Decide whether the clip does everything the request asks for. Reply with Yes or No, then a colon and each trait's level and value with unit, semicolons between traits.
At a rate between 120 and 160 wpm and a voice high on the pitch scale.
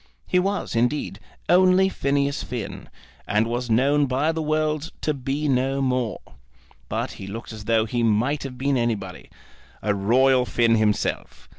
No: average, 155 wpm; low, 130 Hz